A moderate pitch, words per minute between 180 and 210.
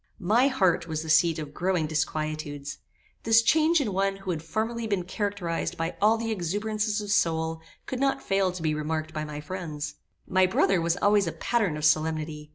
Yes: medium, 175 Hz; average, 190 wpm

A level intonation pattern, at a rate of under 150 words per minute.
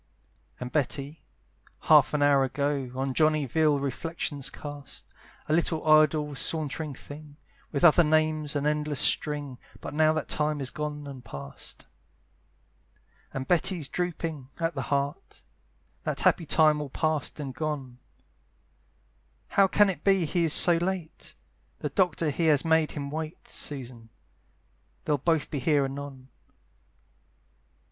Yes: narrow, 2.2 semitones; average, 140 wpm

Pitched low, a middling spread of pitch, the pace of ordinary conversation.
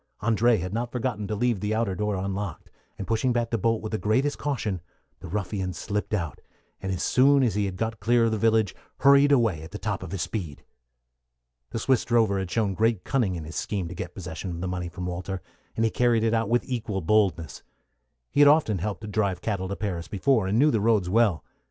No: low, 105 Hz; average, 3.6 semitones; fast, 230 wpm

